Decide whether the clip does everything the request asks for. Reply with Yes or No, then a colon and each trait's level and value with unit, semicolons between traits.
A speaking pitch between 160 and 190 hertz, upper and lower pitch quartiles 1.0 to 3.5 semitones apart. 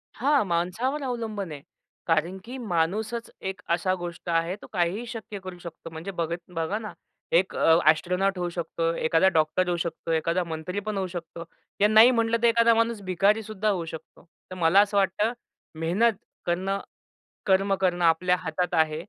No: medium, 185 Hz; average, 4.1 semitones